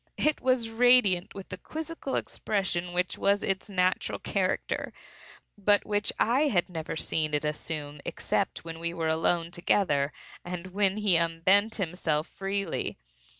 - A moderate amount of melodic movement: Yes, average, 3.8 semitones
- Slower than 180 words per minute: Yes, average, 145 wpm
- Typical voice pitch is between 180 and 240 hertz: Yes, medium, 185 Hz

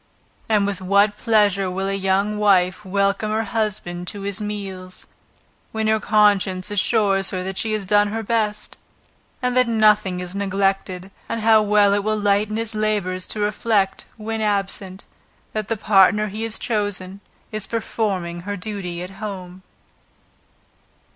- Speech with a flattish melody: Yes, narrow, 1.9 semitones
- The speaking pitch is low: No, high, 205 Hz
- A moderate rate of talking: Yes, average, 150 wpm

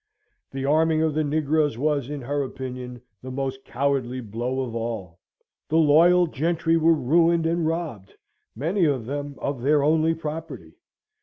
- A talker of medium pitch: Yes, medium, 145 Hz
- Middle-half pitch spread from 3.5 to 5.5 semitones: Yes, average, 3.9 semitones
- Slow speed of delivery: No, average, 155 wpm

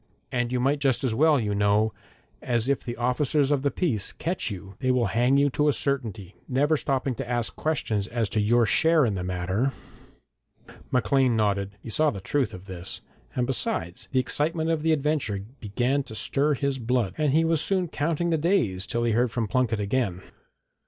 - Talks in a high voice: No, low, 125 Hz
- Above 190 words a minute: Yes, average, 200 wpm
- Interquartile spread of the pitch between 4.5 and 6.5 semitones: Yes, average, 5.1 semitones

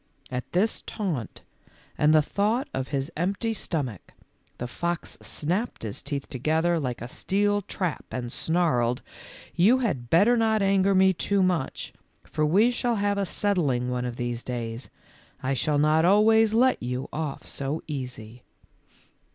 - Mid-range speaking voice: Yes, medium, 160 Hz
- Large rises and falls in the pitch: Yes, wide, 7.9 semitones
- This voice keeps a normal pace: Yes, average, 160 wpm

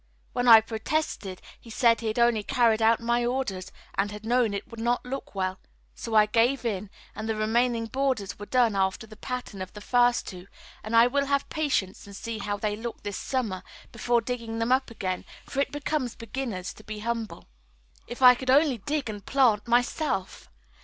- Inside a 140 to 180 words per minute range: No, average, 200 wpm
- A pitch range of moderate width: Yes, average, 3.0 semitones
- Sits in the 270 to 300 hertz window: No, high, 230 Hz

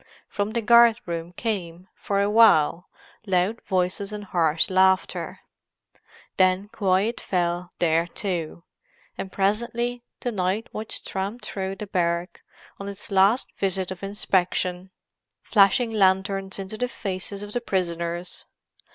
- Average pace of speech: No, slow, 130 wpm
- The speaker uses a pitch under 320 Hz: Yes, high, 190 Hz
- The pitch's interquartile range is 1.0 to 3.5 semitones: Yes, narrow, 2.6 semitones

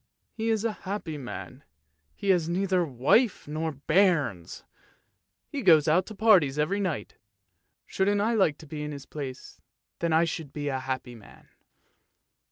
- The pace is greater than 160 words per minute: No, average, 155 wpm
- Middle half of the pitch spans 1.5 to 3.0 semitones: No, wide, 5.4 semitones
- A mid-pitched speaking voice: Yes, medium, 160 Hz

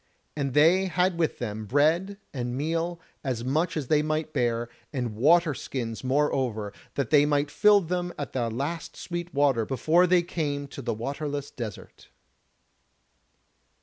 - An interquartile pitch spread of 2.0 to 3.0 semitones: No, average, 5.1 semitones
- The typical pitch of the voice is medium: Yes, medium, 145 Hz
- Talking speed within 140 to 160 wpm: Yes, average, 150 wpm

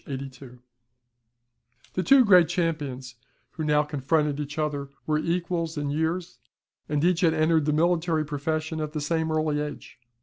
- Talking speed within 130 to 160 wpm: Yes, average, 155 wpm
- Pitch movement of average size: No, narrow, 2.1 semitones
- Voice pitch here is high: No, medium, 155 Hz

